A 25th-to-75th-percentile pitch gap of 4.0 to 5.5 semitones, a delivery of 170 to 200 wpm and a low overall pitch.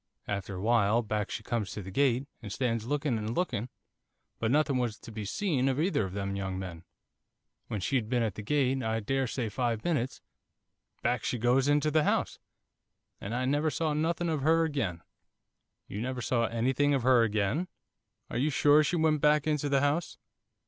Yes: average, 5.1 semitones; average, 190 wpm; low, 125 Hz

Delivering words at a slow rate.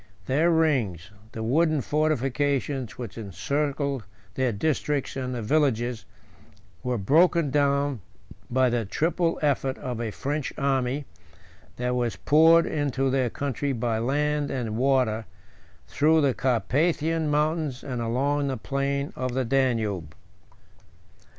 Yes: slow, 120 wpm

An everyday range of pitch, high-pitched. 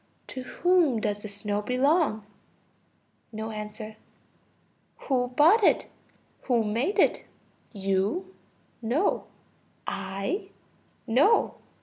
No: wide, 6.4 semitones; high, 235 Hz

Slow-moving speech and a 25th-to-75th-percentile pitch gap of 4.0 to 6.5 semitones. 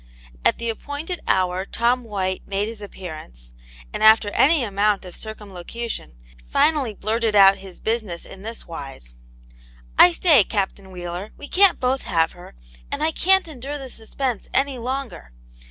No: average, 155 wpm; wide, 5.4 semitones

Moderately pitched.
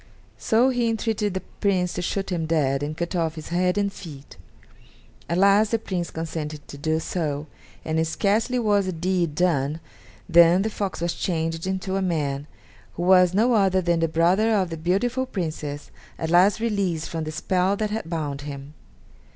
Yes: medium, 175 Hz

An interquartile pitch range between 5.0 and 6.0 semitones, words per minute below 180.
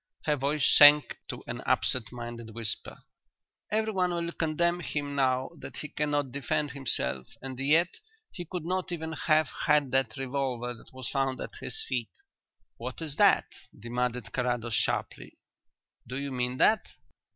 No: average, 4.1 semitones; average, 150 wpm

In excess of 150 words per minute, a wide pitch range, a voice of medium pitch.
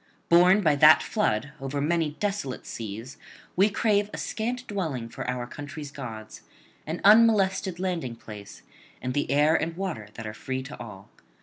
Yes: average, 170 wpm; wide, 7.1 semitones; medium, 150 Hz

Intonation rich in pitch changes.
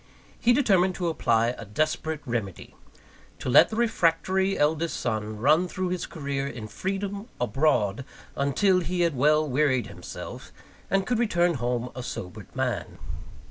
Yes: wide, 6.9 semitones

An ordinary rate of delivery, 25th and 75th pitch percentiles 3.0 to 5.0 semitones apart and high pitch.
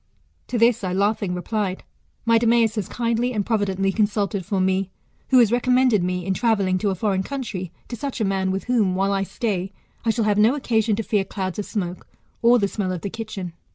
No: fast, 215 wpm; average, 3.3 semitones; high, 205 Hz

